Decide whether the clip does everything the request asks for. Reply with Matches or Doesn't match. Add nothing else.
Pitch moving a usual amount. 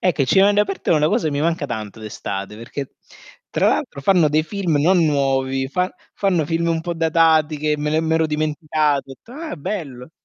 Matches